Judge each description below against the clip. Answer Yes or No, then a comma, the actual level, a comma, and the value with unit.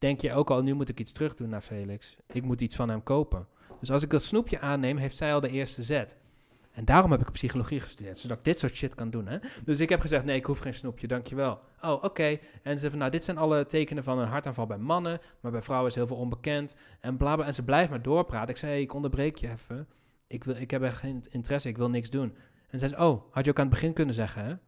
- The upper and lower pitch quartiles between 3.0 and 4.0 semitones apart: Yes, average, 3.3 semitones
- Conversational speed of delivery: No, fast, 275 wpm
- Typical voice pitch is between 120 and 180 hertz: Yes, low, 135 Hz